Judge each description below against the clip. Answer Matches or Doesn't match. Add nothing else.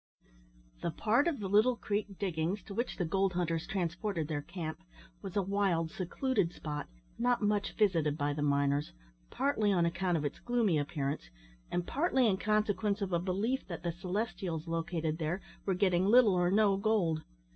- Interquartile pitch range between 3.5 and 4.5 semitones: Matches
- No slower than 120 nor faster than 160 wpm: Doesn't match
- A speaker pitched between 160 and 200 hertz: Matches